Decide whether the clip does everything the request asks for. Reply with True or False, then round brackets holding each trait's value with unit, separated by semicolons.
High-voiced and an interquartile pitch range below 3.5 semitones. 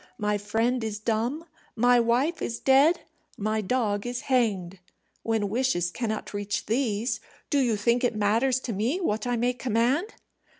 True (230 Hz; 3.1 semitones)